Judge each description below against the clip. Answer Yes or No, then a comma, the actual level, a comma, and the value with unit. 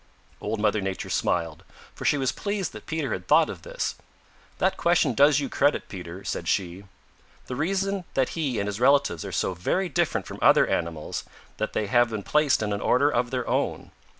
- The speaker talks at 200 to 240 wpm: Yes, fast, 205 wpm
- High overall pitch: No, low, 125 Hz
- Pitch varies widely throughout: Yes, wide, 7.1 semitones